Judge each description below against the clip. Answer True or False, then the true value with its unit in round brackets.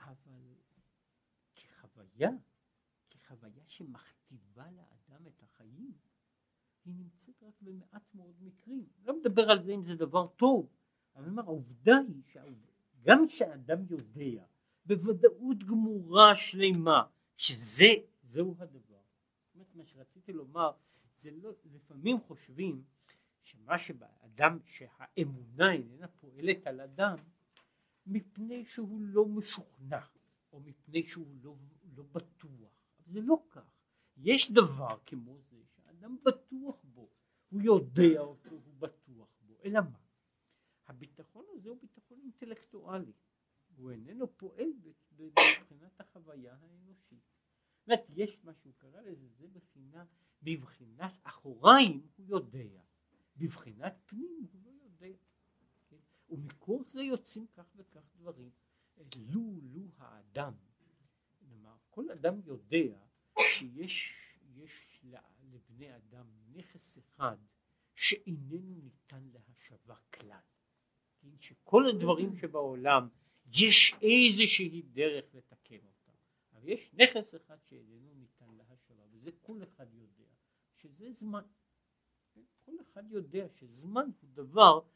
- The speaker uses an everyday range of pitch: False (7.2 semitones)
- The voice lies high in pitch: False (165 Hz)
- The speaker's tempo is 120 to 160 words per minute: False (110 wpm)